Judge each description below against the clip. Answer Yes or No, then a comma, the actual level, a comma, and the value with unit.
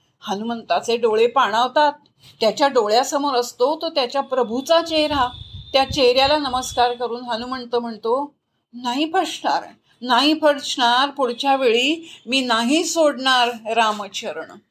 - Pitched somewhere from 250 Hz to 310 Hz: Yes, very high, 255 Hz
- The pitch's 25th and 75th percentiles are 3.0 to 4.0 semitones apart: Yes, average, 3.6 semitones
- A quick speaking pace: No, average, 105 wpm